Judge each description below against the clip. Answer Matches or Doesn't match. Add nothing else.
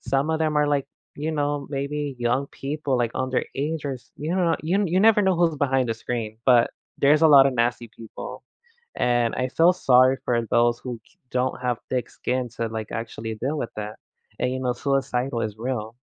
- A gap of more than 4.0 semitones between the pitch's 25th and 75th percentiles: Doesn't match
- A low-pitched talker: Matches